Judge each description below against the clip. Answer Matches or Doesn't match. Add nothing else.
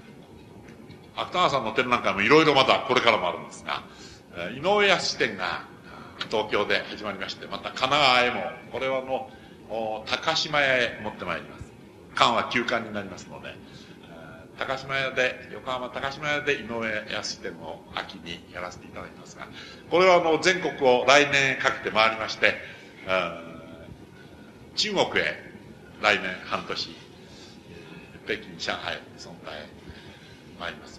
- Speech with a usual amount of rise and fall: Matches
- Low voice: Matches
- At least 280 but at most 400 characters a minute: Doesn't match